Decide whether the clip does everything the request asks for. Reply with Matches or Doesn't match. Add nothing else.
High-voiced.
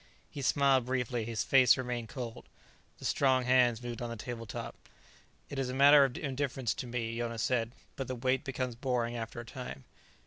Doesn't match